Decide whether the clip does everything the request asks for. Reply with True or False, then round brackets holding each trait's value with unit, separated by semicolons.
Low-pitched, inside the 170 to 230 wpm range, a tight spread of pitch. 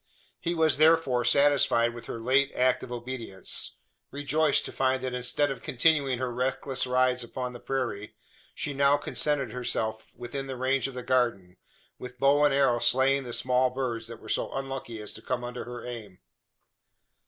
True (130 Hz; 175 wpm; 2.2 semitones)